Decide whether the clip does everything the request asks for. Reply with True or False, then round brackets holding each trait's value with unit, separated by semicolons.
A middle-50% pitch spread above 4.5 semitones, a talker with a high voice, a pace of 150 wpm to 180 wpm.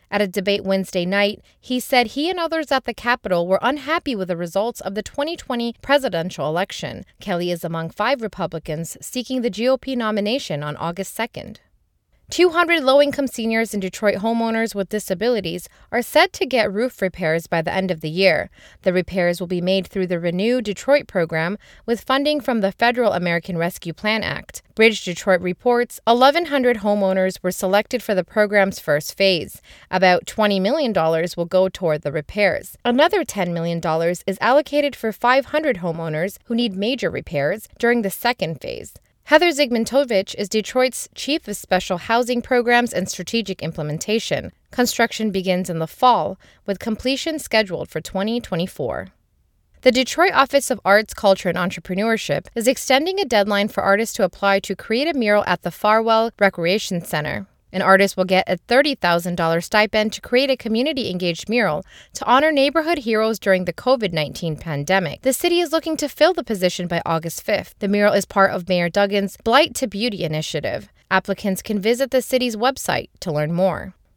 True (5.3 semitones; 205 Hz; 170 wpm)